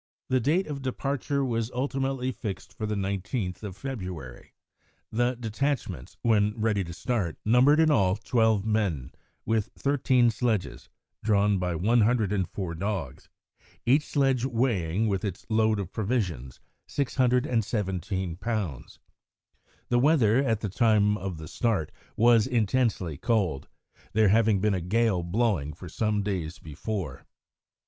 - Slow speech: Yes, slow, 130 wpm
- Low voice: Yes, low, 110 Hz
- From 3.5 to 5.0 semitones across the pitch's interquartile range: Yes, average, 4.4 semitones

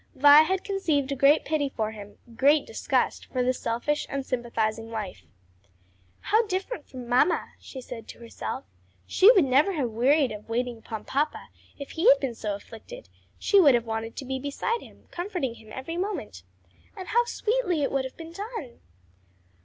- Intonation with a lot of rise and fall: Yes, wide, 6.9 semitones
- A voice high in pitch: Yes, very high, 275 Hz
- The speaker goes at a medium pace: Yes, average, 175 wpm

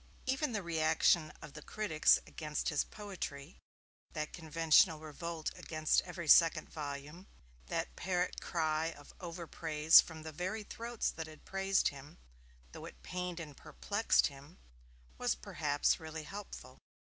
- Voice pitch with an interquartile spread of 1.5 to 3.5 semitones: Yes, average, 2.9 semitones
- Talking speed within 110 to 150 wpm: Yes, average, 140 wpm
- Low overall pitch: No, medium, 160 Hz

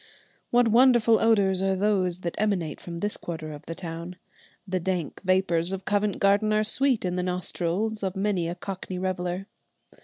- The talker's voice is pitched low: No, high, 190 Hz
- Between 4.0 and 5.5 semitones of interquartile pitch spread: No, average, 2.9 semitones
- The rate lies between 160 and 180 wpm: Yes, average, 175 wpm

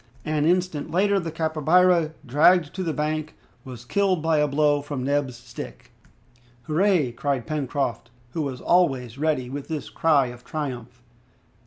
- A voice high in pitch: No, medium, 150 Hz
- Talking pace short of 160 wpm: Yes, average, 150 wpm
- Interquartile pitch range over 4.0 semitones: No, average, 3.6 semitones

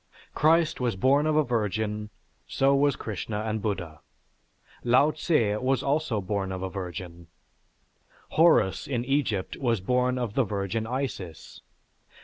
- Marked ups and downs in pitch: Yes, wide, 5.8 semitones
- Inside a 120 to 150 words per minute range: Yes, slow, 135 wpm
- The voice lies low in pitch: Yes, low, 115 Hz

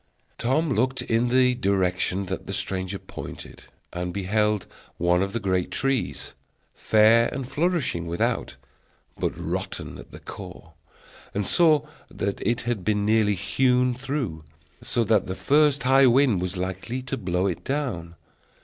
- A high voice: No, low, 110 Hz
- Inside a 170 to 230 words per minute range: No, average, 150 wpm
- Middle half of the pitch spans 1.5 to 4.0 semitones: No, wide, 5.6 semitones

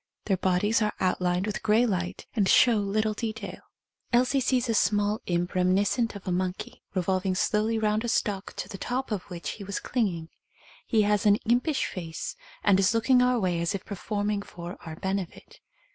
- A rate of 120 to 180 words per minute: No, average, 190 wpm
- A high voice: Yes, high, 205 Hz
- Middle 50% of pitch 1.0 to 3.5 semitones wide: Yes, average, 3.2 semitones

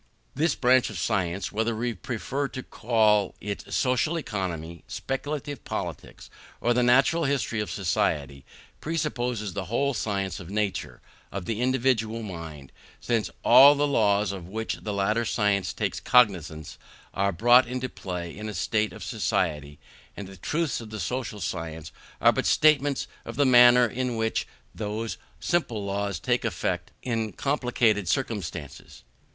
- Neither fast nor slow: Yes, average, 150 wpm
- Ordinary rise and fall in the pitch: Yes, average, 4.3 semitones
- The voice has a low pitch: Yes, low, 110 Hz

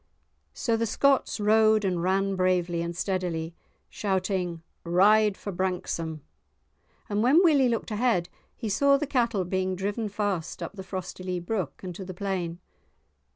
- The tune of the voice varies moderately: Yes, average, 3.2 semitones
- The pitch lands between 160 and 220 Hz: Yes, high, 190 Hz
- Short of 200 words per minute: Yes, average, 150 wpm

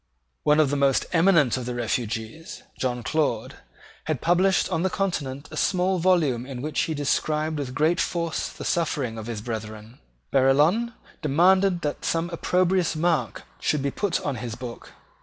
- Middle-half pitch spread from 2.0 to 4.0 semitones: No, wide, 5.5 semitones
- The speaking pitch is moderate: Yes, medium, 150 Hz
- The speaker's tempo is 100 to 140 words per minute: No, average, 165 wpm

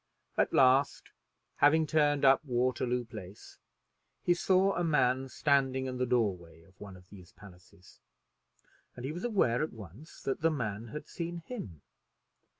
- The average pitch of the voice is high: No, low, 130 Hz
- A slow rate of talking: No, average, 155 wpm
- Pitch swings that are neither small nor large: No, wide, 6.6 semitones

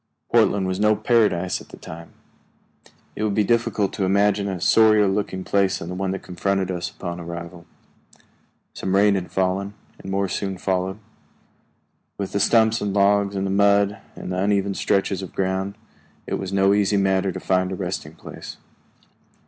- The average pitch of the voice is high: No, very low, 95 Hz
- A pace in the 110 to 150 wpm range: No, average, 175 wpm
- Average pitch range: No, narrow, 1.5 semitones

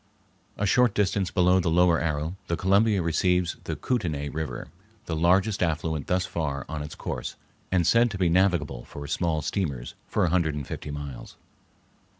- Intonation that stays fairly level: No, average, 3.5 semitones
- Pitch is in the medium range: No, very low, 85 Hz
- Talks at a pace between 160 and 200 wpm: Yes, average, 170 wpm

